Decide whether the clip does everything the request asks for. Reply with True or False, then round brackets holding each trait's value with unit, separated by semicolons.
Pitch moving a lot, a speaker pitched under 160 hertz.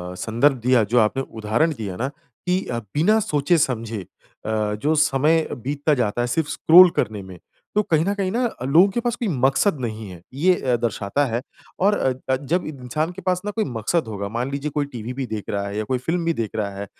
True (6.7 semitones; 135 Hz)